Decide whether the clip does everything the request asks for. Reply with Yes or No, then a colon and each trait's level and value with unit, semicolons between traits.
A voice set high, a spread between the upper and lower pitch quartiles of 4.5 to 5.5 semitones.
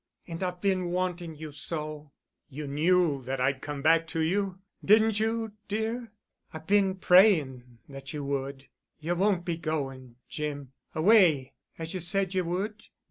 No: medium, 165 Hz; average, 4.9 semitones